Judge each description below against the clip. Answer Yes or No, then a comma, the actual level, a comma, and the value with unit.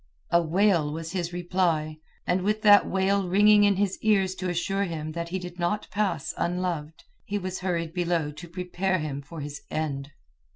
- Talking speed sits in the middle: Yes, average, 180 wpm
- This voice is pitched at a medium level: Yes, medium, 175 Hz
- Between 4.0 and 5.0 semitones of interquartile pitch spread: No, average, 2.9 semitones